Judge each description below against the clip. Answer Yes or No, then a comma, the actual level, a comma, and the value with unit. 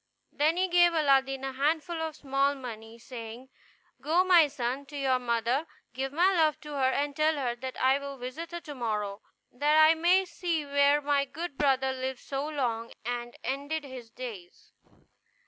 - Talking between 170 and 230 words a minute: Yes, average, 180 wpm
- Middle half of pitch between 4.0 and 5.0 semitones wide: No, average, 3.5 semitones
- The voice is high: Yes, very high, 275 Hz